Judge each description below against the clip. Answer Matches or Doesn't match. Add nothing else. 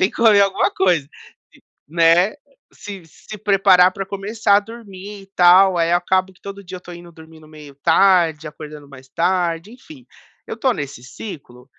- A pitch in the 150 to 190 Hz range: Matches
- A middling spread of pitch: Matches